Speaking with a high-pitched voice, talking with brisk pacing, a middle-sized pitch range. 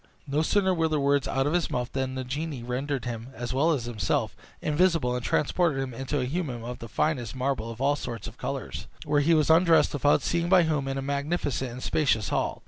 No: medium, 140 Hz; fast, 225 wpm; average, 3.9 semitones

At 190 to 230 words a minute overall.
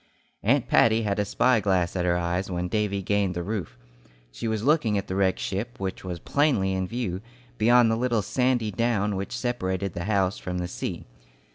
Yes: average, 200 wpm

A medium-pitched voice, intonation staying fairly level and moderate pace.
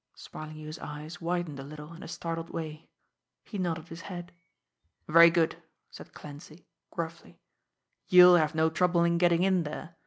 Yes: medium, 165 Hz; narrow, 2.1 semitones; average, 155 wpm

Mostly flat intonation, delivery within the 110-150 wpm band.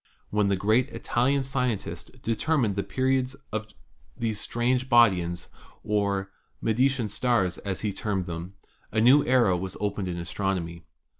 No: average, 4.7 semitones; average, 140 wpm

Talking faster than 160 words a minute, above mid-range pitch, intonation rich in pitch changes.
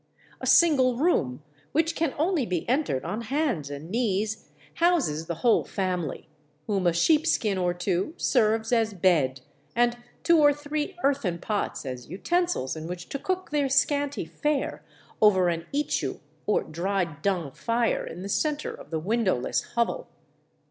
No: average, 155 wpm; high, 220 Hz; wide, 8.8 semitones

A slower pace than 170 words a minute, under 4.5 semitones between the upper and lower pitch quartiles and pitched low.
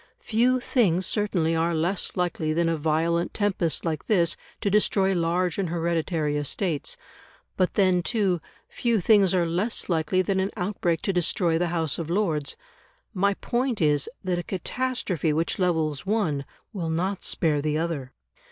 No: average, 160 wpm; average, 3.2 semitones; medium, 175 Hz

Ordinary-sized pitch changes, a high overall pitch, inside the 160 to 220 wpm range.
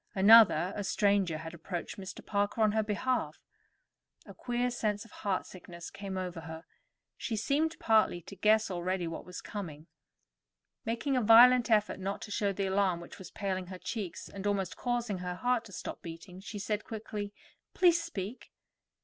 Yes: average, 3.4 semitones; high, 200 Hz; average, 170 wpm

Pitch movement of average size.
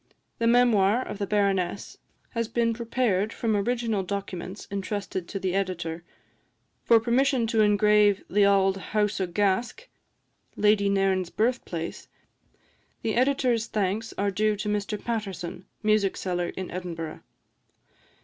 Yes: average, 3.0 semitones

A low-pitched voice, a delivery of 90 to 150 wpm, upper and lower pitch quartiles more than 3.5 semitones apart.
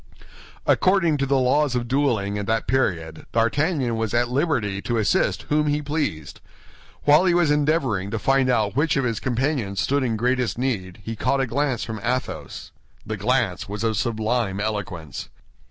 No: low, 120 Hz; average, 170 wpm; average, 4.7 semitones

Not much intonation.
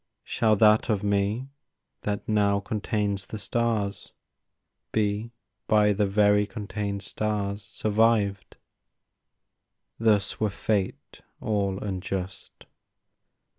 Yes: narrow, 1.3 semitones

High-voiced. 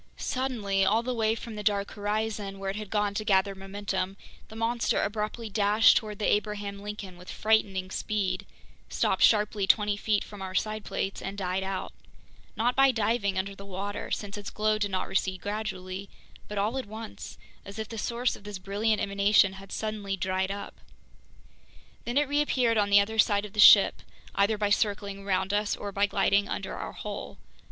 Yes: high, 205 Hz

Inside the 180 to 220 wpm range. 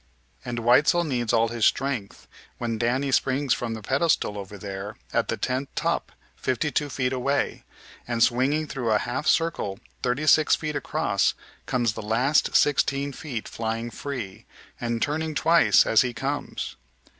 No: average, 155 wpm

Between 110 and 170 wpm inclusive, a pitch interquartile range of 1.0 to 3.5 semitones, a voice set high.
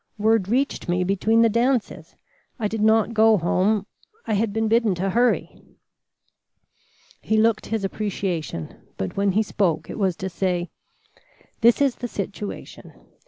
Yes: average, 150 wpm; average, 2.9 semitones; high, 210 Hz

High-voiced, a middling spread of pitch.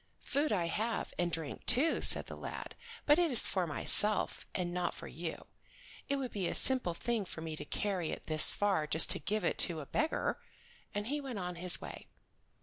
No: high, 195 Hz; wide, 6.0 semitones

